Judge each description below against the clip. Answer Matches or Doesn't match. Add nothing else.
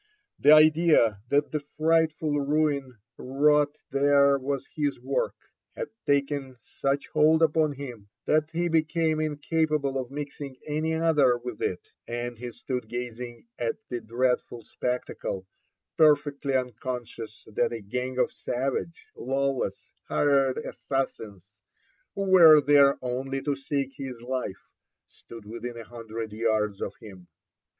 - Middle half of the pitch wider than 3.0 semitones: Matches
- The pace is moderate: Doesn't match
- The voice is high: Doesn't match